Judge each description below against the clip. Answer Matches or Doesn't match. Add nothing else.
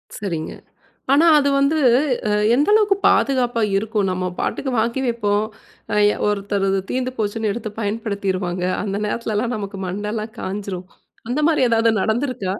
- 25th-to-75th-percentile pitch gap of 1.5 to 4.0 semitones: Matches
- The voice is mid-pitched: Doesn't match